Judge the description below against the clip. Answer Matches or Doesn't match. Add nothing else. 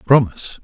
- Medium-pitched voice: Doesn't match